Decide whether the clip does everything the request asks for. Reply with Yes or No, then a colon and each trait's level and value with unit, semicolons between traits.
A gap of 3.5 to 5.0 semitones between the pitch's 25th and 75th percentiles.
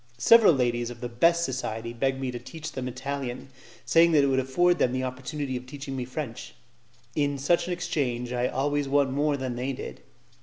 No: average, 2.7 semitones